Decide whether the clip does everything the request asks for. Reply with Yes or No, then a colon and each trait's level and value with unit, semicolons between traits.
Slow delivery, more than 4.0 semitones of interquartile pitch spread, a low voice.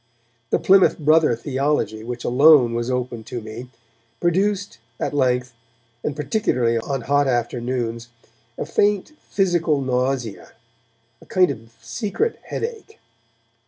Yes: slow, 120 wpm; wide, 5.4 semitones; low, 130 Hz